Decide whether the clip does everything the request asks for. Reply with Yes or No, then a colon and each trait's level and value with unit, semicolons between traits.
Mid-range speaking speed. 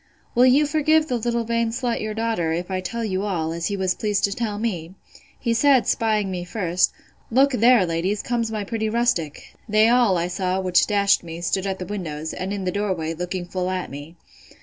No: fast, 215 wpm